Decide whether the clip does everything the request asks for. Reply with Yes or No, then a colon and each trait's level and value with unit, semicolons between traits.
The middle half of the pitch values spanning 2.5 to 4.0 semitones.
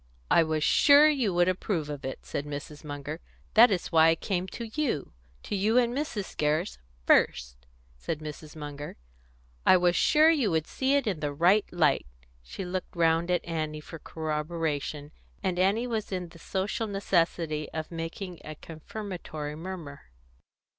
No: average, 4.5 semitones